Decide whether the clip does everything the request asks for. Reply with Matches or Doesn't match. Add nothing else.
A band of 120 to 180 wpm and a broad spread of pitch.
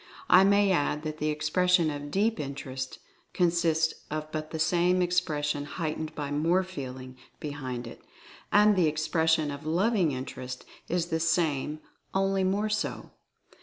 Doesn't match